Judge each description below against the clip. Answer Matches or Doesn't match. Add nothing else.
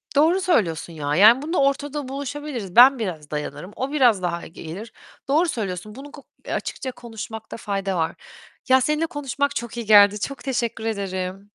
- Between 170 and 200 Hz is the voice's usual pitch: Doesn't match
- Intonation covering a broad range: Matches